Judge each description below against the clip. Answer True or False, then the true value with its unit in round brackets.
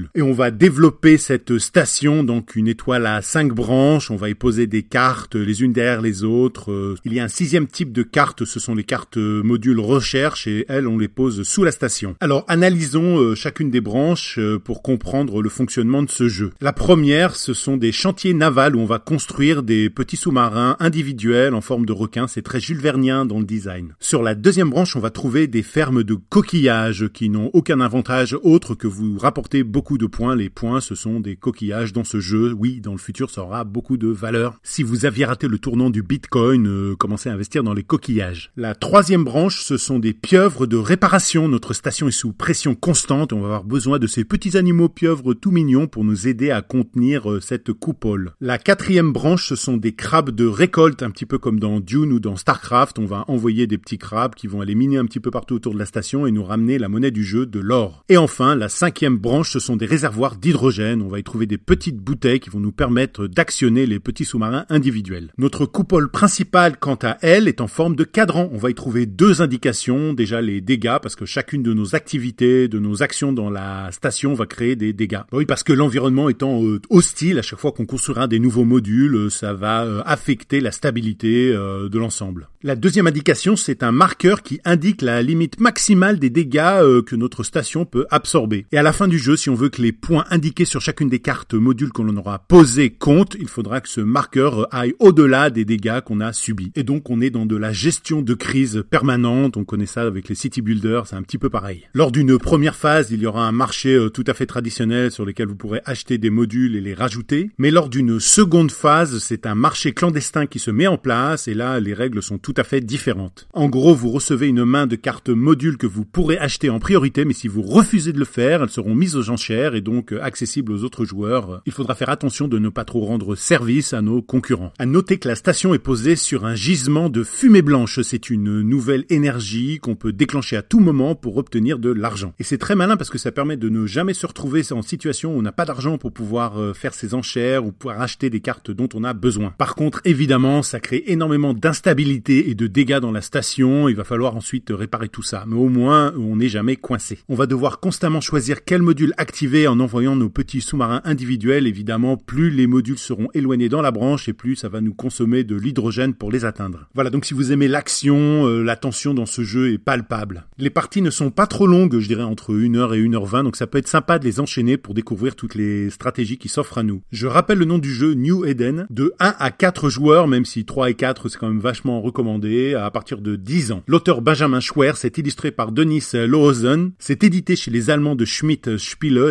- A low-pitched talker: True (125 Hz)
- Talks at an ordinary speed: False (225 wpm)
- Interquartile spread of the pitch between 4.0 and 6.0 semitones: True (4.5 semitones)